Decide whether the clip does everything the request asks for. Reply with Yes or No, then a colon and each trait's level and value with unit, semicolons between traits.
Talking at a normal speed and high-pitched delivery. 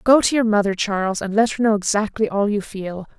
No: fast, 245 wpm; high, 210 Hz